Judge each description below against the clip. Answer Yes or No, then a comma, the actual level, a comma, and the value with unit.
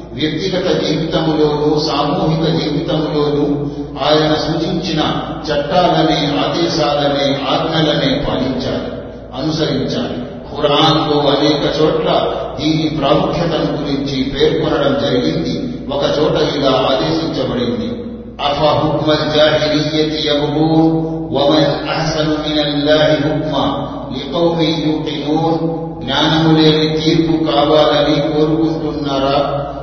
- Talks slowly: Yes, slow, 50 wpm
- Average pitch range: No, narrow, 1.3 semitones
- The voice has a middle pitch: Yes, medium, 150 Hz